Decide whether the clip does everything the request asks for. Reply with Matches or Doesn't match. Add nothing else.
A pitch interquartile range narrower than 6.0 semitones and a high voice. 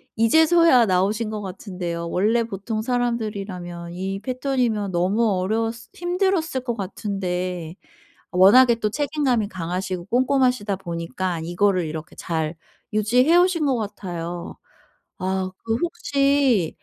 Matches